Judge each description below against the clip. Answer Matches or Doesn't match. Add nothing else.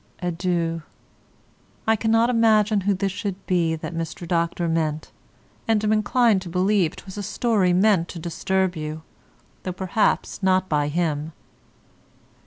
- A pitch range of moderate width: Matches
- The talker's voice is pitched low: Doesn't match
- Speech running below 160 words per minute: Matches